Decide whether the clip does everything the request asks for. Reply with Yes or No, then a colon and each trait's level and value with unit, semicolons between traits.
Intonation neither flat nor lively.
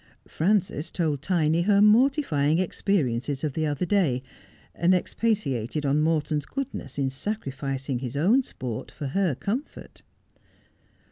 No: wide, 6.4 semitones